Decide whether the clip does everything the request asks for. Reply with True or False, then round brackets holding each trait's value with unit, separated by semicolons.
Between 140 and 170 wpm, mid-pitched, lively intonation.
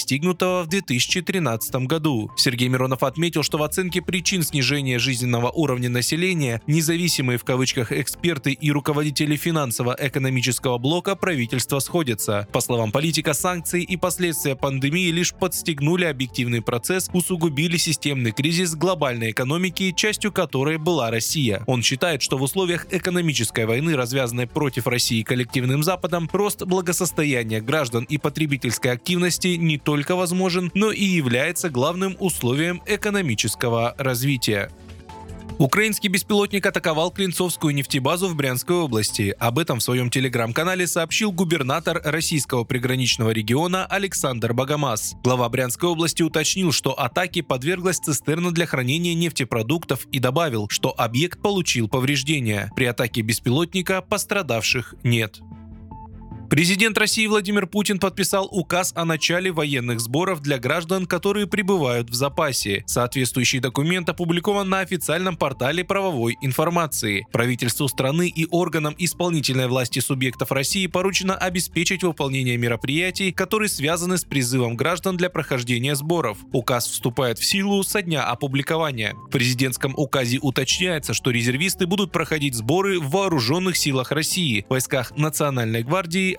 False (125 wpm; 150 Hz; 6.0 semitones)